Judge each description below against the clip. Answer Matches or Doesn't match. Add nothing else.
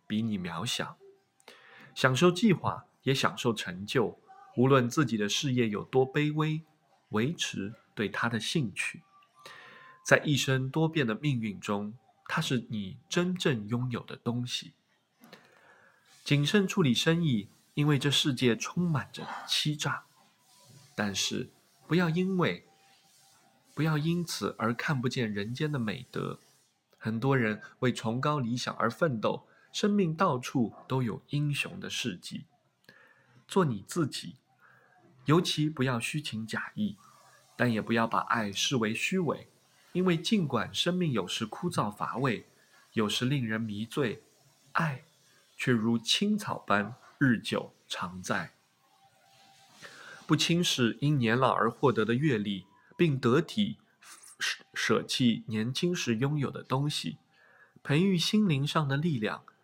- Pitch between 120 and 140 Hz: Matches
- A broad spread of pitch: Matches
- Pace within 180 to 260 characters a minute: Matches